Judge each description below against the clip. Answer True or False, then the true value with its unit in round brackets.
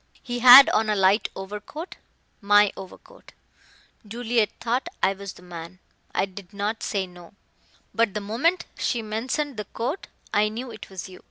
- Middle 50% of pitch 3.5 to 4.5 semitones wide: True (3.9 semitones)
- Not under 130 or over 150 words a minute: False (160 wpm)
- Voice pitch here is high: True (210 Hz)